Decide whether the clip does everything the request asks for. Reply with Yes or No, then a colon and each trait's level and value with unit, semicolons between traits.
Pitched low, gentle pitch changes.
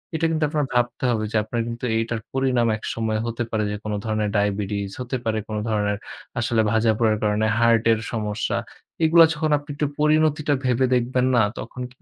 No: low, 115 Hz; average, 3.2 semitones